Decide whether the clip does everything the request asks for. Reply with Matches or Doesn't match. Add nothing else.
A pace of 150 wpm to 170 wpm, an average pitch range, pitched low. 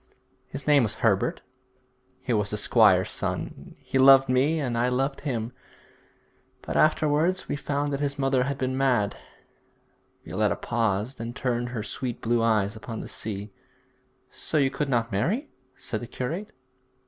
Matches